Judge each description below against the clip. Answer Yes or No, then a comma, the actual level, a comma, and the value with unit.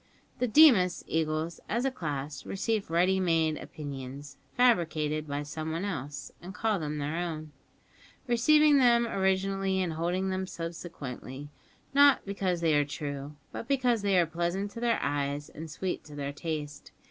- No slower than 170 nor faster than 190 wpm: No, average, 155 wpm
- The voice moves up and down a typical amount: Yes, average, 5.0 semitones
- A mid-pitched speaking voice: Yes, medium, 170 Hz